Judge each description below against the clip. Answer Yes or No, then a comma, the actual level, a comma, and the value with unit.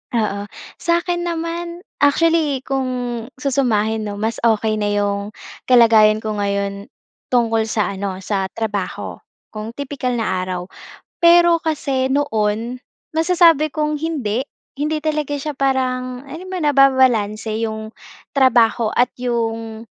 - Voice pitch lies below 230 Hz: No, high, 245 Hz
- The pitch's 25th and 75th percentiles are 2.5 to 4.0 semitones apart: No, average, 5.1 semitones